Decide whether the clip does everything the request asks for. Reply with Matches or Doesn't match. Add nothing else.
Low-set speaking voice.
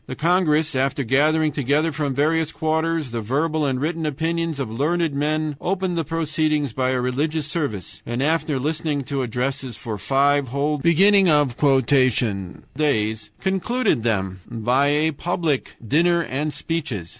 Doesn't match